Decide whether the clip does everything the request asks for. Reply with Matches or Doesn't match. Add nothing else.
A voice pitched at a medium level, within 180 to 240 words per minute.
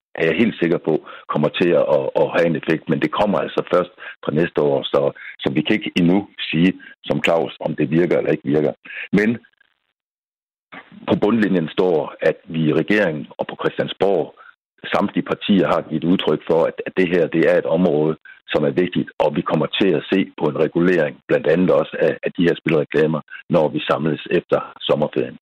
Doesn't match